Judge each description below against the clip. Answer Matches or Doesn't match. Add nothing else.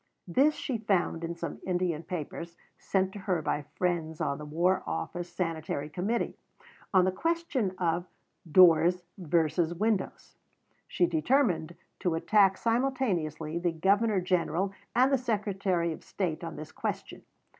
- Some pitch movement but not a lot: Matches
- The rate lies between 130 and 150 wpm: Matches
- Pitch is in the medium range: Matches